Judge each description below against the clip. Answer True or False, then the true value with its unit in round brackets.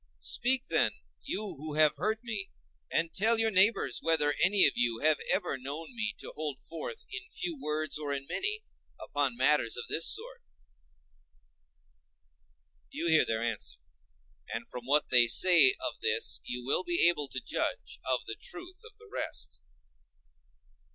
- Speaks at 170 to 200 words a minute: False (160 wpm)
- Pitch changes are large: True (8.6 semitones)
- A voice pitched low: False (165 Hz)